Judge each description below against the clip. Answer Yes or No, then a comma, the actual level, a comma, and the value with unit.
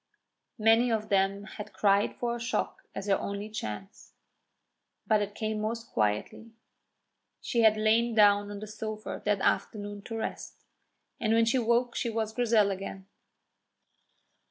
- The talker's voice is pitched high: Yes, high, 215 Hz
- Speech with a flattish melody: Yes, narrow, 2.0 semitones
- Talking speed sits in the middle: Yes, average, 150 wpm